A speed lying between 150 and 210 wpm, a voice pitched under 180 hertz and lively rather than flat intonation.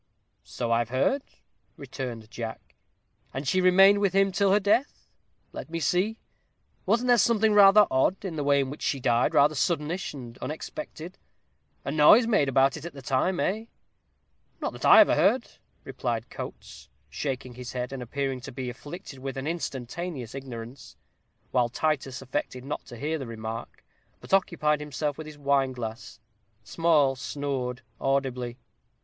Yes: average, 160 wpm; medium, 140 Hz; wide, 5.7 semitones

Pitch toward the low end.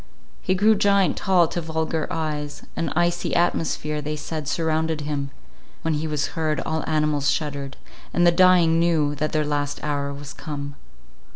No: medium, 155 Hz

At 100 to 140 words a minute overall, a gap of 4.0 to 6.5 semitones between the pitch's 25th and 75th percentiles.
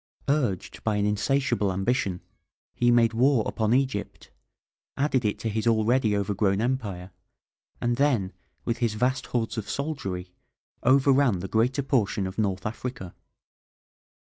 Yes: slow, 135 wpm; average, 4.3 semitones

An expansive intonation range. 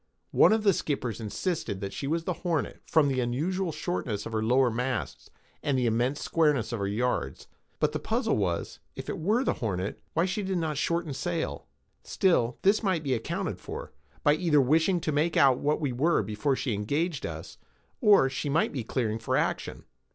Yes: wide, 5.9 semitones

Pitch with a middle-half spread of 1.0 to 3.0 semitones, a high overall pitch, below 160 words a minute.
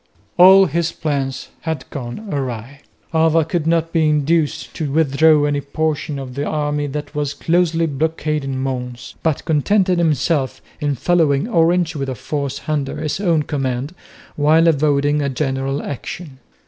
No: average, 2.7 semitones; medium, 150 Hz; average, 150 wpm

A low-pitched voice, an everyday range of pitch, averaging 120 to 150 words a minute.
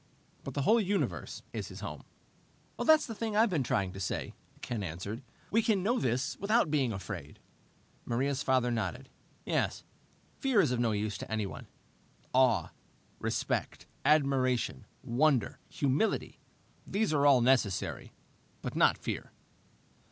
No: low, 130 Hz; wide, 8.5 semitones; average, 140 wpm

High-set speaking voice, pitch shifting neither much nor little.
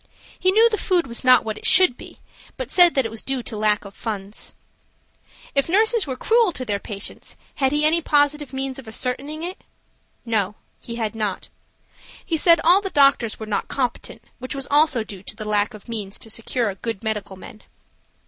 No: very high, 250 Hz; wide, 6.0 semitones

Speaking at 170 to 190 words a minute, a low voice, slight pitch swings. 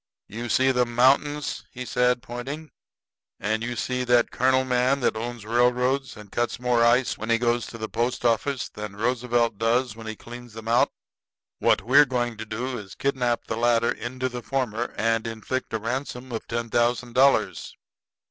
Yes: average, 185 wpm; low, 120 Hz; narrow, 1.8 semitones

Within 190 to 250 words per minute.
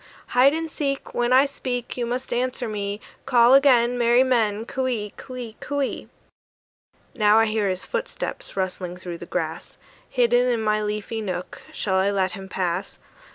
No: average, 175 wpm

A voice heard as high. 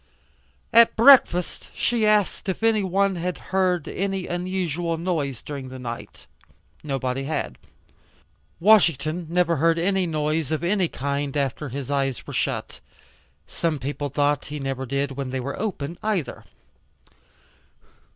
No: medium, 160 Hz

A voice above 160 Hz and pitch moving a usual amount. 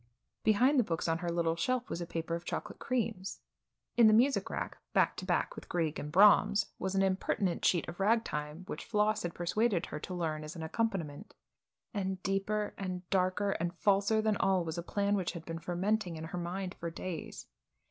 Yes: medium, 185 Hz; average, 3.6 semitones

